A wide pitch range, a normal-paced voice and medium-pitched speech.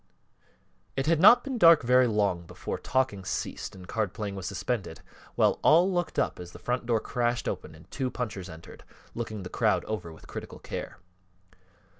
No: wide, 5.7 semitones; average, 180 wpm; low, 115 Hz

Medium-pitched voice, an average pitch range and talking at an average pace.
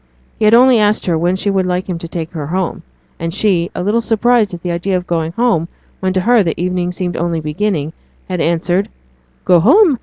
No: medium, 180 Hz; average, 3.8 semitones; fast, 220 wpm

